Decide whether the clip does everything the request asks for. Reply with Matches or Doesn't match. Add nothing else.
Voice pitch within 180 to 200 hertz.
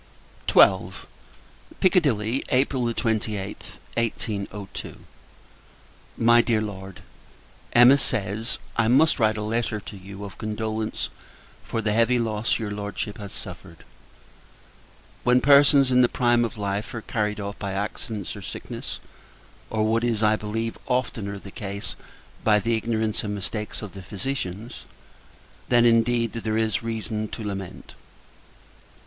Doesn't match